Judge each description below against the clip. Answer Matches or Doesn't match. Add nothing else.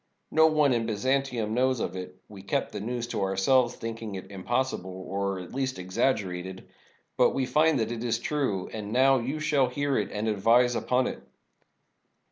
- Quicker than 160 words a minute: Matches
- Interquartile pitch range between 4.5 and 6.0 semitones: Matches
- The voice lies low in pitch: Matches